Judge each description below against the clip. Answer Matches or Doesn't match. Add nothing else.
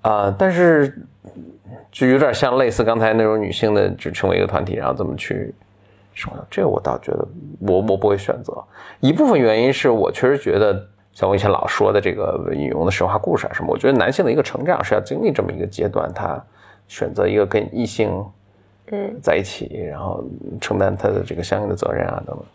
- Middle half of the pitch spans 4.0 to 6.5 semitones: Doesn't match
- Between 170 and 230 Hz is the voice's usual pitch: Doesn't match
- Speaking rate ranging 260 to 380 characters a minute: Matches